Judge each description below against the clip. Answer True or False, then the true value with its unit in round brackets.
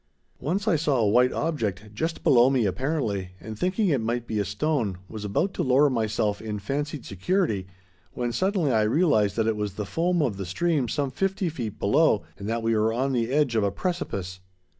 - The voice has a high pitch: False (120 Hz)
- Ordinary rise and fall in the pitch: False (6.3 semitones)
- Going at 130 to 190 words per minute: False (205 wpm)